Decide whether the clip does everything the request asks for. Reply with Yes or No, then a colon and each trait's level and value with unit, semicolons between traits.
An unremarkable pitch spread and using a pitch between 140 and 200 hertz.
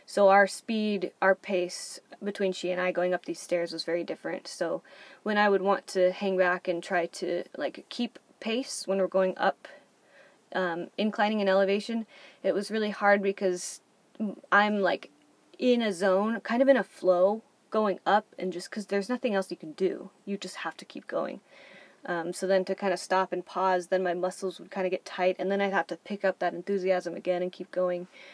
No: narrow, 2.1 semitones; high, 190 Hz